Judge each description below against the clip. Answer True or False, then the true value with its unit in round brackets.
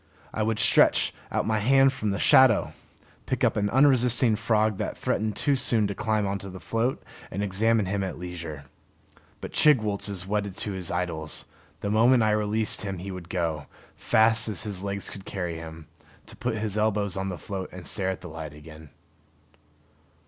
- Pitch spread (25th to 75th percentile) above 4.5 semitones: False (3.2 semitones)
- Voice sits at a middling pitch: False (100 Hz)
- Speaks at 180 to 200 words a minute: True (185 wpm)